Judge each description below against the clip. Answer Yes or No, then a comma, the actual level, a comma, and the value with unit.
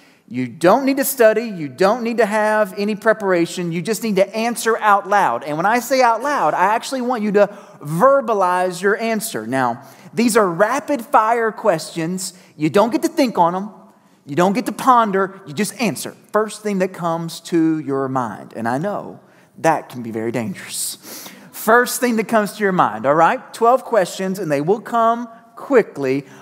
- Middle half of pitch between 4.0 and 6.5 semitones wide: Yes, average, 4.4 semitones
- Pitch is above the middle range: Yes, high, 205 Hz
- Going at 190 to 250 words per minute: Yes, average, 195 wpm